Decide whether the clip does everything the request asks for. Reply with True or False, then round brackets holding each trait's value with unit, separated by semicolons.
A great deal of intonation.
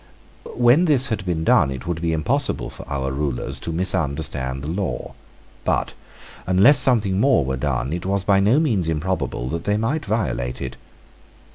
True (7.8 semitones)